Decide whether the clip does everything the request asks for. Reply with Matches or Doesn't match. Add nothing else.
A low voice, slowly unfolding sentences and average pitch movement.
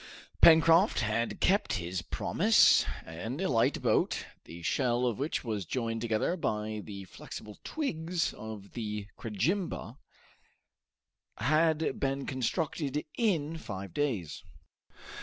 Doesn't match